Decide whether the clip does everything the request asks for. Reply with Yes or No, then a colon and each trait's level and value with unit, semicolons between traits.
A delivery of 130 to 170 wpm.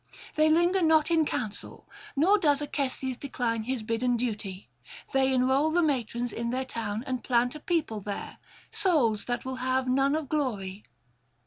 Yes: average, 160 wpm